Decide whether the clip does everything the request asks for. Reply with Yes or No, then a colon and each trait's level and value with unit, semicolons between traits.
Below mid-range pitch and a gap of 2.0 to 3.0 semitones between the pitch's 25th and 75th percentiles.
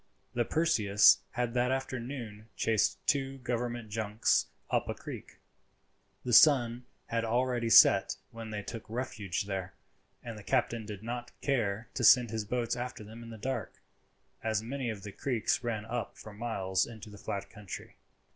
Yes: low, 115 Hz; narrow, 2.6 semitones